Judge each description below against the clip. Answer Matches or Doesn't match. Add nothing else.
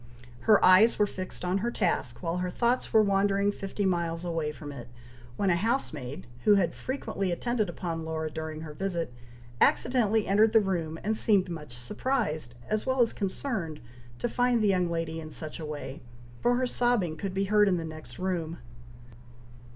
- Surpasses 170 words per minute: Matches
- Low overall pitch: Doesn't match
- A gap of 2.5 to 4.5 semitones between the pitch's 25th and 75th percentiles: Doesn't match